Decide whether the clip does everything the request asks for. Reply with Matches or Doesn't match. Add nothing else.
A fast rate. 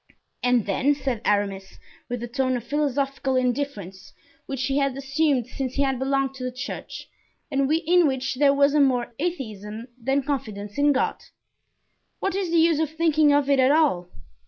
Doesn't match